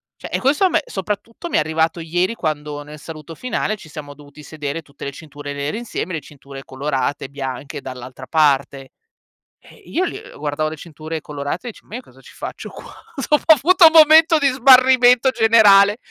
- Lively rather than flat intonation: Yes, wide, 8.9 semitones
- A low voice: No, medium, 160 Hz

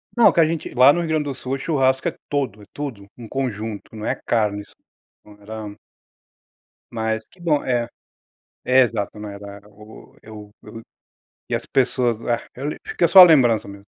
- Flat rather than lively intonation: No, average, 4.5 semitones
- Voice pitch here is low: Yes, low, 115 Hz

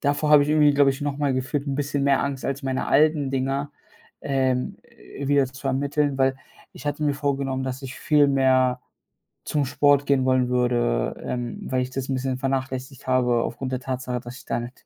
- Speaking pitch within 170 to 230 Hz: No, low, 135 Hz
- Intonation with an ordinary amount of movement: No, narrow, 1.6 semitones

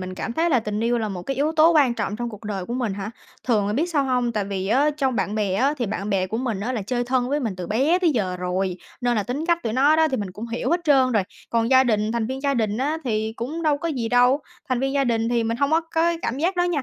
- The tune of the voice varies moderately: Yes, average, 5.0 semitones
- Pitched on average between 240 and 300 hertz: Yes, high, 245 Hz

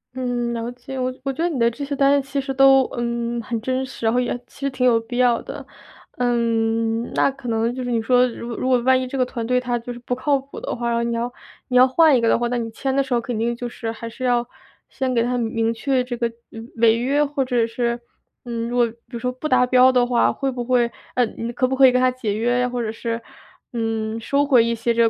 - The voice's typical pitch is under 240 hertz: No, high, 245 Hz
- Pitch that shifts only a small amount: Yes, narrow, 1.7 semitones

